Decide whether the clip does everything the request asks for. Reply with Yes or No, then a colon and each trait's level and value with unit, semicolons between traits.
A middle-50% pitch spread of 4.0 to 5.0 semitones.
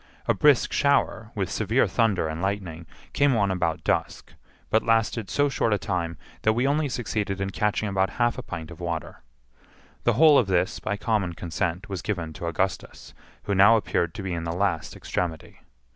Yes: average, 4.7 semitones